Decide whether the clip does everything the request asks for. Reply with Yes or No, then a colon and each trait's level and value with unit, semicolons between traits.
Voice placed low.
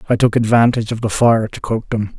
Yes: low, 110 Hz